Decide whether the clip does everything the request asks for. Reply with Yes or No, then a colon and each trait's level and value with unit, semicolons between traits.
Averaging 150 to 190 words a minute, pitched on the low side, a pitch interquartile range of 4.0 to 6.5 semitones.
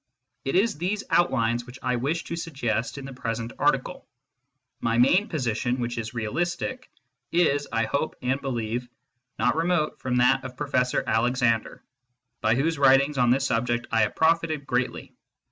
Yes: average, 160 wpm; low, 130 Hz; average, 4.4 semitones